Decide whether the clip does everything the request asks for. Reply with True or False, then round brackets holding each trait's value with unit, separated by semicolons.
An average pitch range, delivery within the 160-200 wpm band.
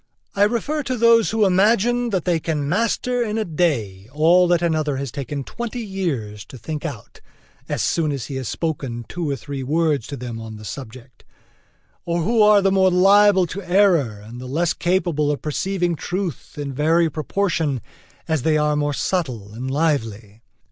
False (5.9 semitones; 180 wpm)